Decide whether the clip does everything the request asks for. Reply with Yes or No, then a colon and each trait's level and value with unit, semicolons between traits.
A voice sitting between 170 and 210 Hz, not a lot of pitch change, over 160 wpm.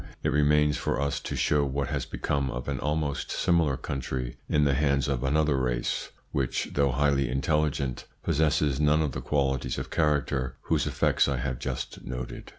No: very low, 70 Hz; narrow, 2.2 semitones; average, 175 wpm